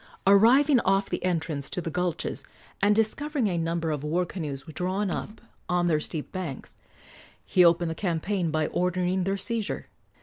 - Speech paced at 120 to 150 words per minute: No, average, 165 wpm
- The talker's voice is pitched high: No, medium, 180 Hz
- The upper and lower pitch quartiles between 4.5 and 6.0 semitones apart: No, average, 3.4 semitones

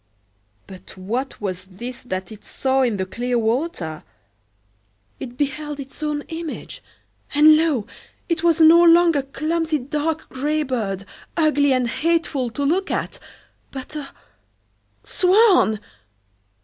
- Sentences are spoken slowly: Yes, slow, 125 wpm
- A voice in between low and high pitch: No, very high, 280 Hz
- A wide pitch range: No, average, 5.0 semitones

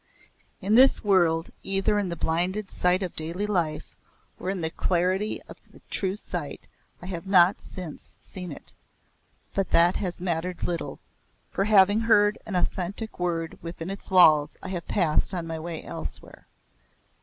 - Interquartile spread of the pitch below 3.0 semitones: Yes, narrow, 2.6 semitones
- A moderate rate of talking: Yes, average, 160 wpm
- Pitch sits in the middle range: Yes, medium, 180 Hz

